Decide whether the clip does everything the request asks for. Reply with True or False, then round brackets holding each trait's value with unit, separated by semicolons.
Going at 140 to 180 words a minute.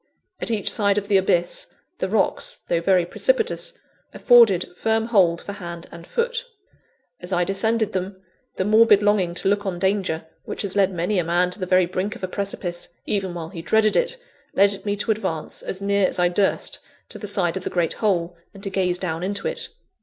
False (205 wpm)